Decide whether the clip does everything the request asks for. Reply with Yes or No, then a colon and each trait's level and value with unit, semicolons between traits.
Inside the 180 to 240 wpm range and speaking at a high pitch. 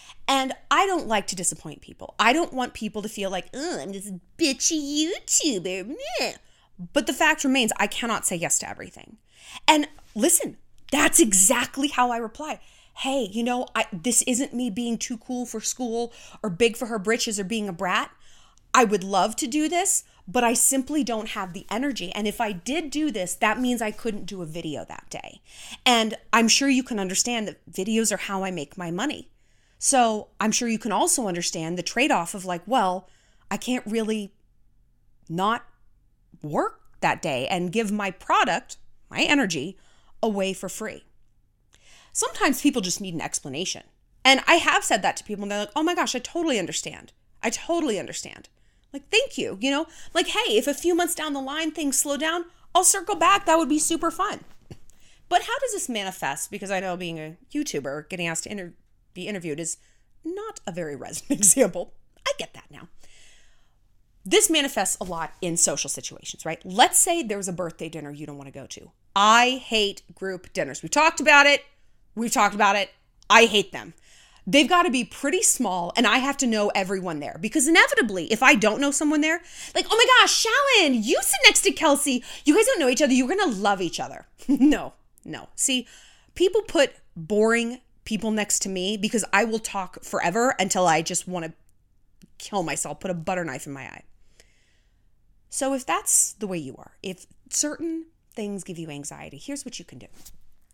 Yes: average, 195 wpm; high, 230 Hz